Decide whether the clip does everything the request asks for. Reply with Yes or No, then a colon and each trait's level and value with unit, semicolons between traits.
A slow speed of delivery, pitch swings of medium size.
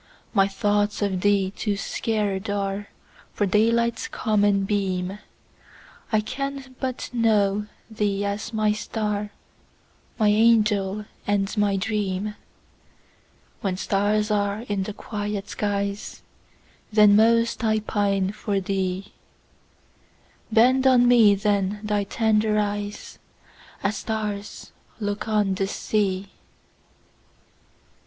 No: slow, 90 wpm; narrow, 1.4 semitones